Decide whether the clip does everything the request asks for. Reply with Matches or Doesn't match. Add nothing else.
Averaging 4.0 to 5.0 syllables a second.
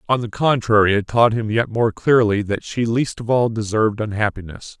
Doesn't match